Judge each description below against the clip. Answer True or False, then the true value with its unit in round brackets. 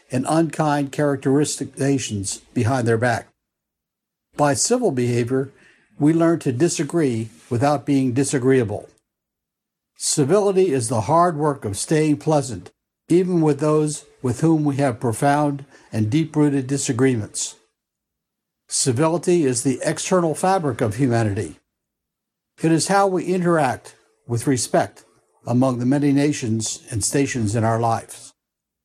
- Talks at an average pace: False (125 wpm)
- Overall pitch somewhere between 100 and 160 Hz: True (140 Hz)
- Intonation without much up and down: False (4.2 semitones)